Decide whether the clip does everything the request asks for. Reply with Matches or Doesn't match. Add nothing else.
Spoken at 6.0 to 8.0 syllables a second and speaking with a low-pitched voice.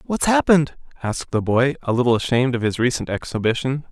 Matches